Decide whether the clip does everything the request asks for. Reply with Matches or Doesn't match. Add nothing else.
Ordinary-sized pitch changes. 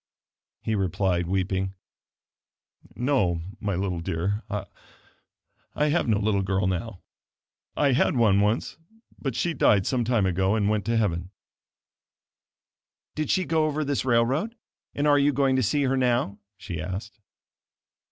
Doesn't match